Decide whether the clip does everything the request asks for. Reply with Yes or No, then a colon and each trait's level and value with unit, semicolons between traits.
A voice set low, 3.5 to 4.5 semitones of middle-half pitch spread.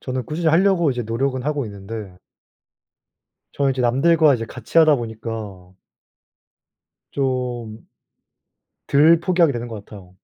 No: low, 125 Hz; average, 5.2 semitones